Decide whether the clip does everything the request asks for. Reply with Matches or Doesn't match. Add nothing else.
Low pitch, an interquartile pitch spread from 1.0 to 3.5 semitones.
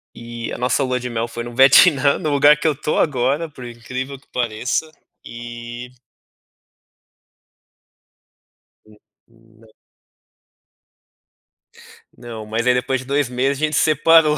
Matches